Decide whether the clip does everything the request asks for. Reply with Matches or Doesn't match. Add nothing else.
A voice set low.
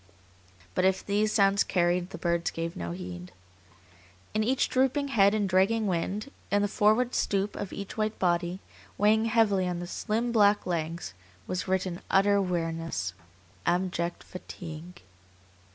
Doesn't match